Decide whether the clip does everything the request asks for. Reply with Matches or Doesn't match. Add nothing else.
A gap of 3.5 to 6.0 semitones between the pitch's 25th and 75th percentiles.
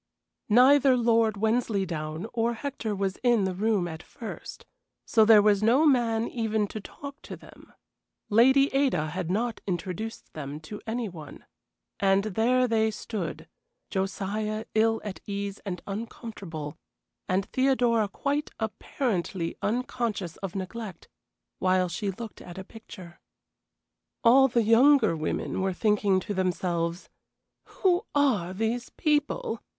Matches